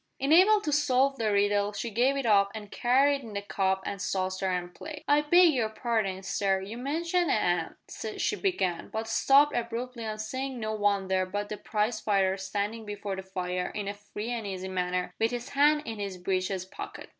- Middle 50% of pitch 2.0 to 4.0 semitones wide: No, average, 4.9 semitones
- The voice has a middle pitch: No, high, 210 Hz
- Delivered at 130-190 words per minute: No, average, 200 wpm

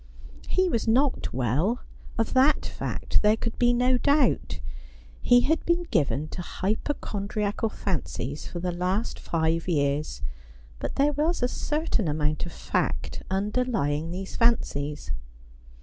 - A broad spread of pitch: Yes, wide, 7.7 semitones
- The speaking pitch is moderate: No, high, 210 Hz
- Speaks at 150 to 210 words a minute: No, slow, 135 wpm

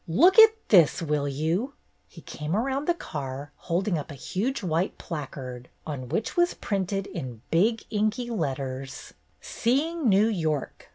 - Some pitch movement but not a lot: No, wide, 8.1 semitones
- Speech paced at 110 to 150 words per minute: No, average, 160 wpm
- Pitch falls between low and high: Yes, medium, 180 Hz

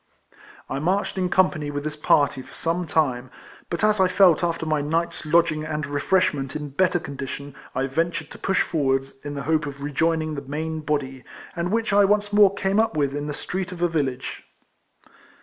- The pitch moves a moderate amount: Yes, average, 3.8 semitones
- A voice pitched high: No, medium, 155 Hz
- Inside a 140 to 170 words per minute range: No, average, 195 wpm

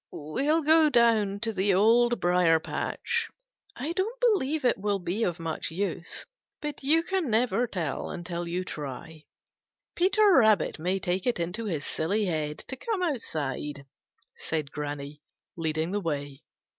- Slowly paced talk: No, average, 150 wpm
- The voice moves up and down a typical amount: No, wide, 7.8 semitones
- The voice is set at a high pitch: Yes, high, 195 Hz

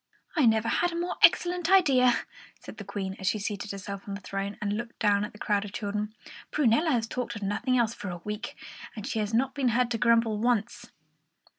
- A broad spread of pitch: No, average, 3.3 semitones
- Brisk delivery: Yes, fast, 230 wpm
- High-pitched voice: Yes, high, 220 Hz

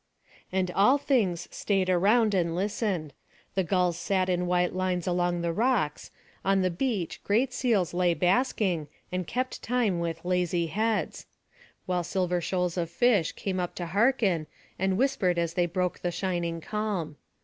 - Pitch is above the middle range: No, medium, 180 Hz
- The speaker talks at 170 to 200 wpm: No, average, 160 wpm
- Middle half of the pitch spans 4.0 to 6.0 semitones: No, average, 2.9 semitones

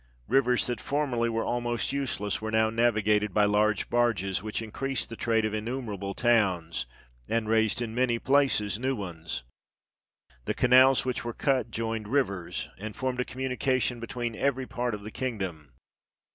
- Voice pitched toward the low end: Yes, low, 115 Hz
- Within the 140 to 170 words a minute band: Yes, average, 160 wpm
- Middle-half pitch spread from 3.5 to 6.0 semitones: No, average, 3.0 semitones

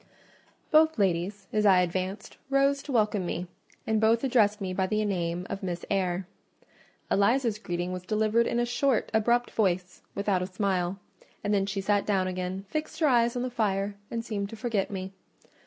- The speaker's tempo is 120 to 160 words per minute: No, average, 185 wpm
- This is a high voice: Yes, high, 205 Hz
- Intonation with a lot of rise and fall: No, average, 3.8 semitones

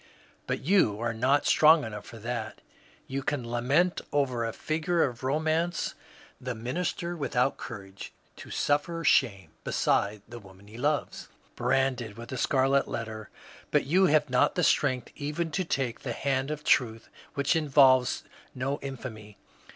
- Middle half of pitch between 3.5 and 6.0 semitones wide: Yes, average, 4.3 semitones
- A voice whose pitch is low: Yes, low, 130 Hz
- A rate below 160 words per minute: Yes, average, 150 wpm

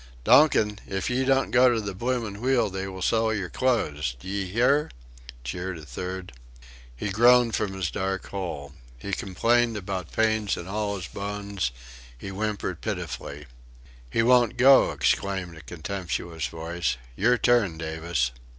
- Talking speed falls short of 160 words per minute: Yes, average, 150 wpm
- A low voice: Yes, low, 100 Hz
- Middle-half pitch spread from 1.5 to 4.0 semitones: No, average, 4.7 semitones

